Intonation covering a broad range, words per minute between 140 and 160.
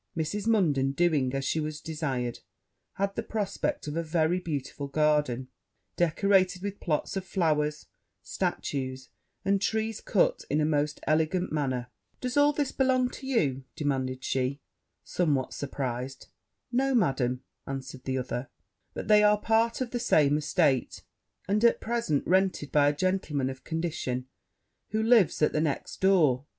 Yes: wide, 6.5 semitones; average, 150 wpm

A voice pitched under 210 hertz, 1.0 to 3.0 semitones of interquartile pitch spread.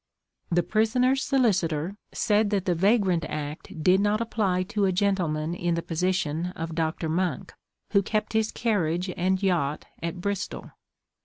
No: medium, 185 Hz; average, 3.8 semitones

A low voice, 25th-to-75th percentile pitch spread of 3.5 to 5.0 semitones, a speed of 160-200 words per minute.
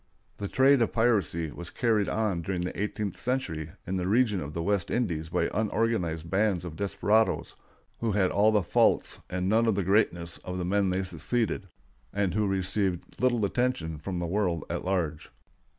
Yes: very low, 95 Hz; average, 3.8 semitones; average, 185 wpm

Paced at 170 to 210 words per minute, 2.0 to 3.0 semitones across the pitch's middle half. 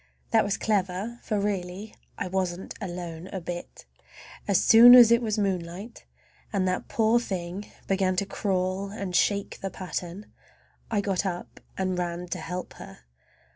No: average, 155 wpm; narrow, 2.4 semitones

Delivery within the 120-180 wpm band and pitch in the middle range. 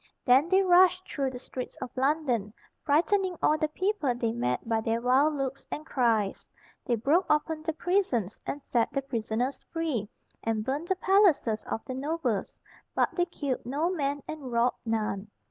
No: average, 175 wpm; very high, 275 Hz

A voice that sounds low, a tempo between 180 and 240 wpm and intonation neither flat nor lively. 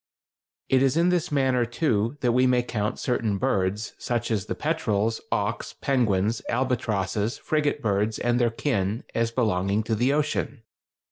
No: low, 115 Hz; average, 155 wpm; average, 3.7 semitones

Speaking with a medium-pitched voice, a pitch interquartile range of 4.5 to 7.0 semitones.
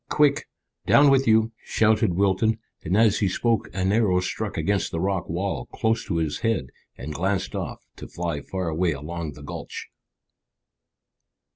No: very low, 95 Hz; average, 4.8 semitones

